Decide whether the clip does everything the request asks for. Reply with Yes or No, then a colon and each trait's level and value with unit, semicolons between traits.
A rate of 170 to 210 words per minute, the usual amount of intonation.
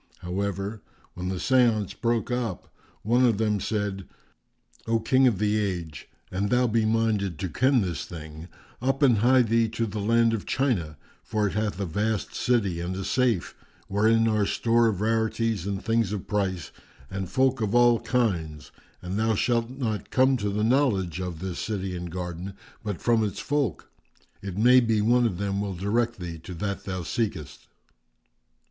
Yes: average, 180 wpm; average, 3.8 semitones